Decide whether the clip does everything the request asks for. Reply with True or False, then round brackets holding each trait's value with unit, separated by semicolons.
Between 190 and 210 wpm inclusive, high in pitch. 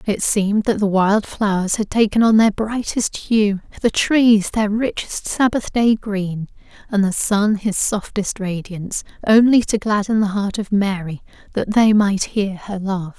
False (175 wpm; 205 Hz)